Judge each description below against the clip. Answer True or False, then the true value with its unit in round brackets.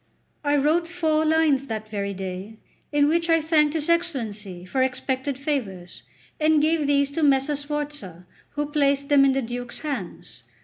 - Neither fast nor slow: True (165 wpm)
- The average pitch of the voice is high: True (280 Hz)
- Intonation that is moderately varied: True (4.9 semitones)